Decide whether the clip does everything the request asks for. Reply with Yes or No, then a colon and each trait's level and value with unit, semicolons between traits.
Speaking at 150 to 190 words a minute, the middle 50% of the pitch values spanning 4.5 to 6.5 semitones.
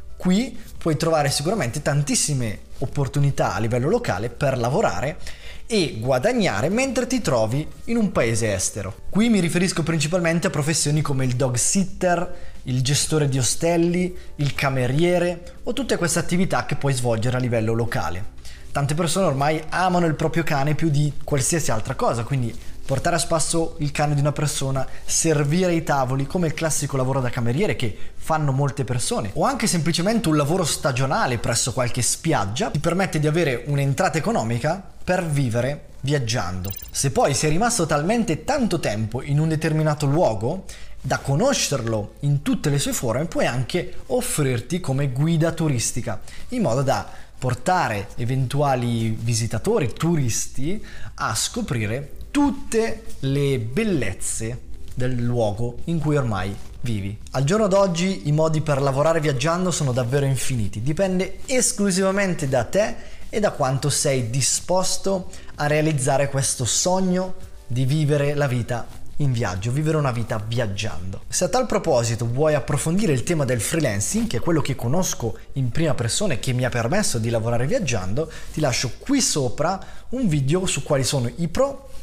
Yes: average, 155 wpm; wide, 5.5 semitones